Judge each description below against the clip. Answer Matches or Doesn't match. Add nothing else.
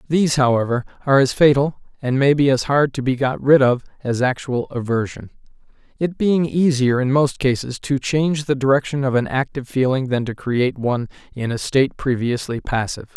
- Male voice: Matches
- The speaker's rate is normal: Matches